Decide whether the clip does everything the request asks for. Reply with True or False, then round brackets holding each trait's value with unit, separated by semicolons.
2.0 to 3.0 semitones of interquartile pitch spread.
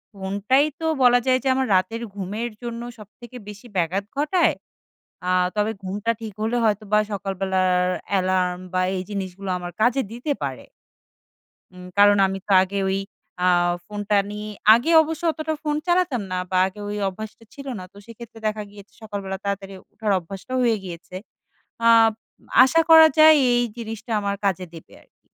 False (3.8 semitones)